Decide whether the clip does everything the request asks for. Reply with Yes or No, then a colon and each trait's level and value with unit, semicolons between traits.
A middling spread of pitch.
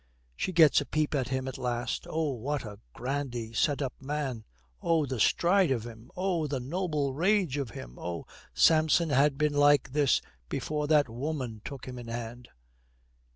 Yes: average, 3.8 semitones